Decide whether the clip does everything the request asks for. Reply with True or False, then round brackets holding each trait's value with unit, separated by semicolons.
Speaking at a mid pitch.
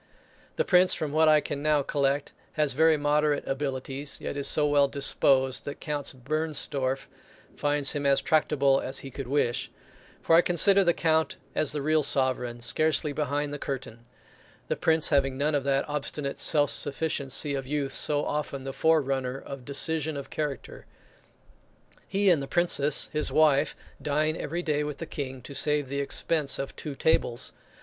True (145 Hz)